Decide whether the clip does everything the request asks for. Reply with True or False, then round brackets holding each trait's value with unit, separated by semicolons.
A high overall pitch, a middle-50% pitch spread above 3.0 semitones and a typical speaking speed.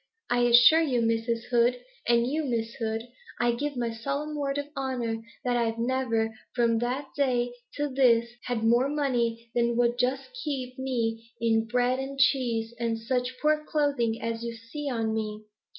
False (240 Hz; 2.6 semitones; 180 wpm)